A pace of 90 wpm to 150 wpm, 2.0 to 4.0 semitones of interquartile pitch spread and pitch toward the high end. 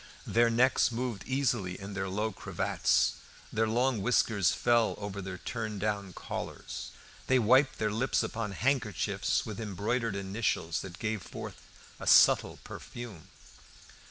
No: slow, 135 wpm; average, 3.3 semitones; low, 110 Hz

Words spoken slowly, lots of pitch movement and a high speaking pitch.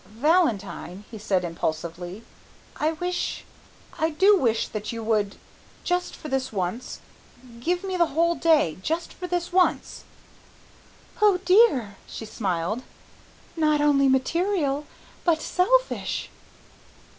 Yes: slow, 120 wpm; wide, 8.8 semitones; very high, 290 Hz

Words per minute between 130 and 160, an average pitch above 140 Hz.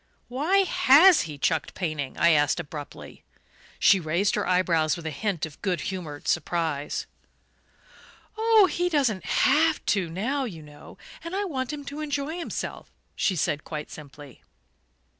Yes: average, 150 wpm; medium, 185 Hz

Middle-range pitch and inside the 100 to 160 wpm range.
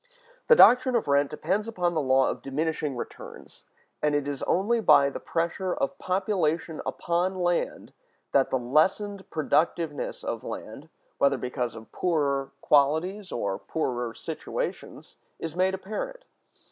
Yes: medium, 160 Hz; average, 140 wpm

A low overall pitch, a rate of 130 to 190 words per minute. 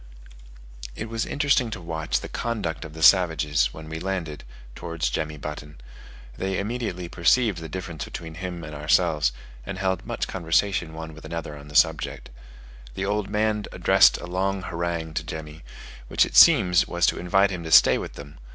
Yes: very low, 85 Hz; average, 180 wpm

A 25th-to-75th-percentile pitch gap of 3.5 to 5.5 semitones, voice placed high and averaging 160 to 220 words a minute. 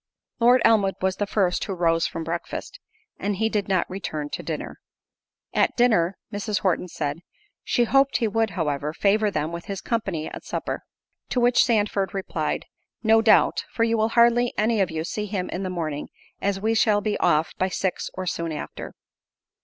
Yes: average, 4.4 semitones; high, 195 Hz; average, 185 wpm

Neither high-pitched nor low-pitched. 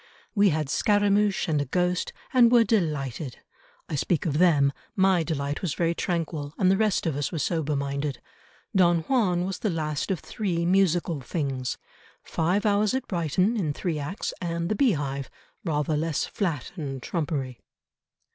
Yes: medium, 170 Hz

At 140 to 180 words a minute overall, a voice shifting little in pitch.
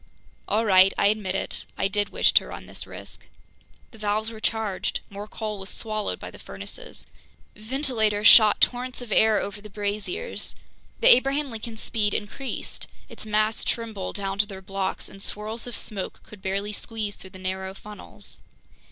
Yes: average, 170 wpm; narrow, 2.0 semitones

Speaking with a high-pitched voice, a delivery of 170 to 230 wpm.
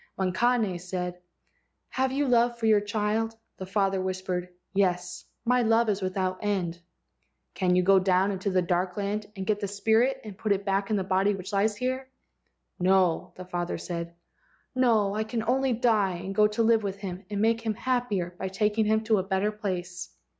Yes: high, 200 Hz; average, 195 wpm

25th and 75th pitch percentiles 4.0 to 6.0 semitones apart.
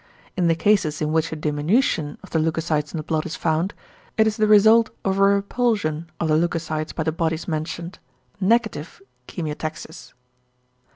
Yes: average, 4.3 semitones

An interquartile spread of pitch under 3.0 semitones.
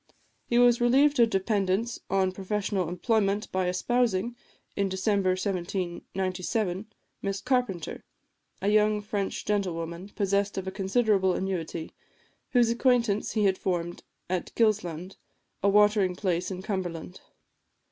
Yes: narrow, 2.5 semitones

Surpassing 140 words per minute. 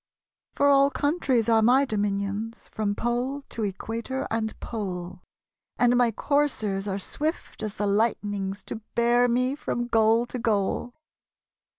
No: slow, 135 wpm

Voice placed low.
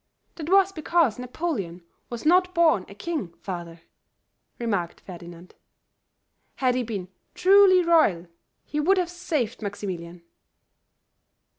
No: very high, 250 Hz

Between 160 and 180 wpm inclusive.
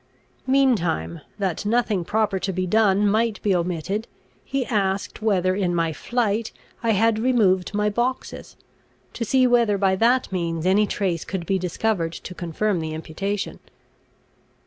No: average, 145 wpm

